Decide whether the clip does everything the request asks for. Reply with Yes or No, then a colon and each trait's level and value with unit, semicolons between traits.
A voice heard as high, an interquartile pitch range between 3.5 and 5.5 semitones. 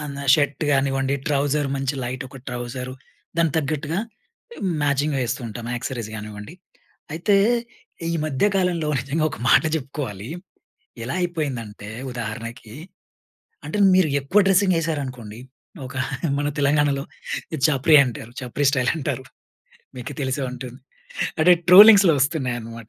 No: medium, 140 Hz; average, 3.9 semitones